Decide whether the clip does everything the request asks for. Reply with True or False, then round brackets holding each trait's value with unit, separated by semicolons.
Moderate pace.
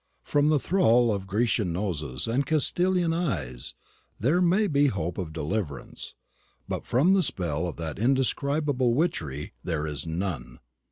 True (145 wpm)